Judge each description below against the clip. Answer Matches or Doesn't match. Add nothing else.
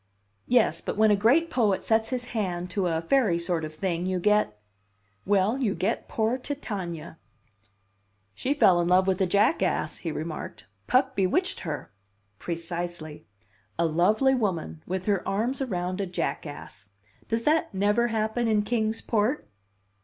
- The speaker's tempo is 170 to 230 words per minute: Doesn't match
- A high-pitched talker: Matches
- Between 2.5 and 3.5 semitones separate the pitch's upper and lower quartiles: Doesn't match